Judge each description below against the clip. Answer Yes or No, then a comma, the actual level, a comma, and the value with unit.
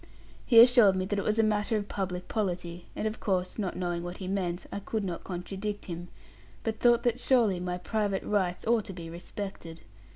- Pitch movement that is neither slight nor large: Yes, average, 3.2 semitones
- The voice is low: No, high, 195 Hz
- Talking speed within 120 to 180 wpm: No, fast, 205 wpm